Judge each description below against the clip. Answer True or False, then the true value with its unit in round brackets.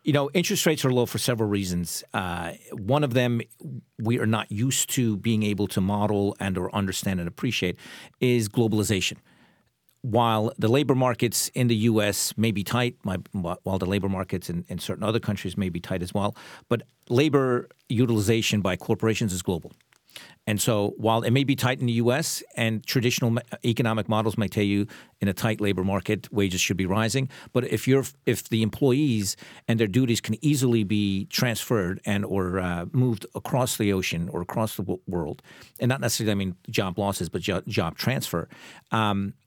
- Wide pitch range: False (3.6 semitones)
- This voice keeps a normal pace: True (185 wpm)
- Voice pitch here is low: True (110 Hz)